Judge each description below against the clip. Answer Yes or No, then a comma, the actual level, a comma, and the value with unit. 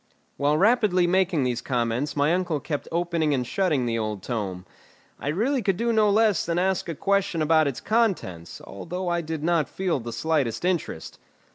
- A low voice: No, medium, 165 Hz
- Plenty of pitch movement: Yes, wide, 6.3 semitones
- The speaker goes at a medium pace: Yes, average, 180 wpm